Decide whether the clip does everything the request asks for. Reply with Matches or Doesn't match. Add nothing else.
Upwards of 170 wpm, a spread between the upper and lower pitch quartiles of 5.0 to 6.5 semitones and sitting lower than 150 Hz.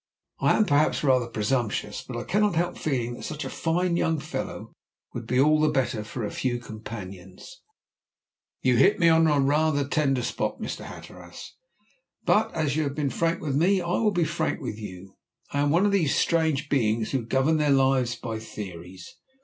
Matches